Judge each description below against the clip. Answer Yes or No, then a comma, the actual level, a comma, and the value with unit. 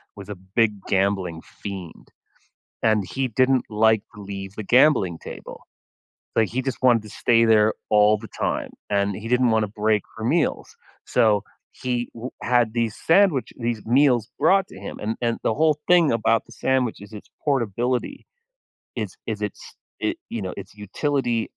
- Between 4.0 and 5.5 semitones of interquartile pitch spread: No, average, 3.4 semitones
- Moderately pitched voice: No, low, 110 Hz